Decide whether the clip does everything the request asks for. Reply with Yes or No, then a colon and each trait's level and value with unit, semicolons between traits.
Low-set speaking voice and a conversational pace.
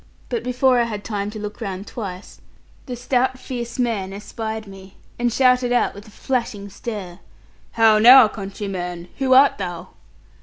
No: high, 220 Hz; average, 160 wpm